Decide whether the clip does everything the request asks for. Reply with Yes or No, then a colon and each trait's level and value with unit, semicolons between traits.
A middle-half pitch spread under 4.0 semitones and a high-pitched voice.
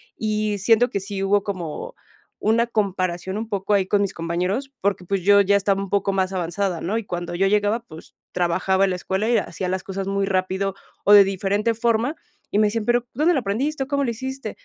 Yes: average, 2.9 semitones; high, 200 Hz